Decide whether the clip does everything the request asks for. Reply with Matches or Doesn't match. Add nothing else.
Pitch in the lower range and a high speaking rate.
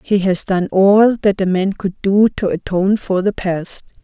Doesn't match